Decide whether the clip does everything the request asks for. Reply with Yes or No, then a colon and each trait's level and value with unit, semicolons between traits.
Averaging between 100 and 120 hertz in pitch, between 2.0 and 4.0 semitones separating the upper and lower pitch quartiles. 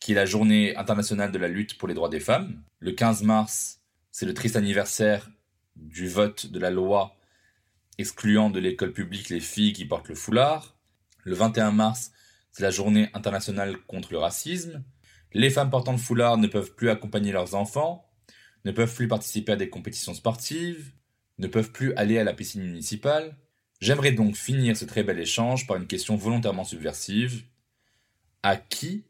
Yes: low, 110 Hz; average, 2.9 semitones